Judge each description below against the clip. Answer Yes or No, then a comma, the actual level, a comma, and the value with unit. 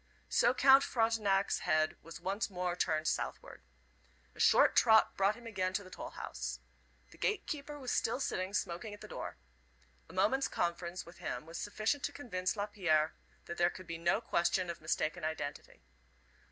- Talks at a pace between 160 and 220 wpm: Yes, average, 170 wpm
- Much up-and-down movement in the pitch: No, average, 4.4 semitones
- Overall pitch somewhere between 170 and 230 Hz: Yes, medium, 185 Hz